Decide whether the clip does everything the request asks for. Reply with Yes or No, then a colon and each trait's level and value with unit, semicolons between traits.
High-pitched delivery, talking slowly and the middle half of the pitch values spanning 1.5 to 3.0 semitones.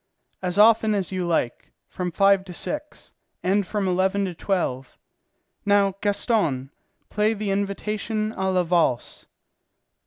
Yes: high, 195 Hz; slow, 130 wpm; narrow, 2.6 semitones